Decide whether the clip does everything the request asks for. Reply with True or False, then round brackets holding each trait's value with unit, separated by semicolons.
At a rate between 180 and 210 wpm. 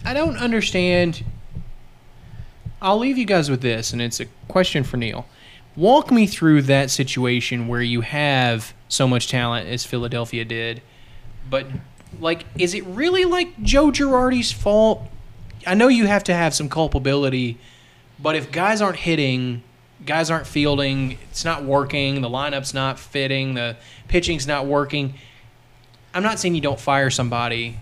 False (155 wpm)